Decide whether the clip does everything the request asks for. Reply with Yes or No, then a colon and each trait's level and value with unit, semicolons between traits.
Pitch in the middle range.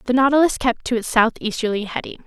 No: high, 240 Hz